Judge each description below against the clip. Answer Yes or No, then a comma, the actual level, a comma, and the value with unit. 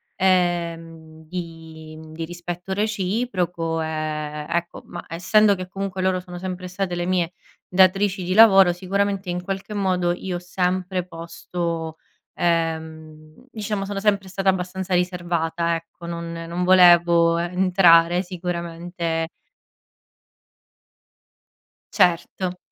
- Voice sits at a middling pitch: Yes, medium, 175 Hz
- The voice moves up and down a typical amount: No, narrow, 2.0 semitones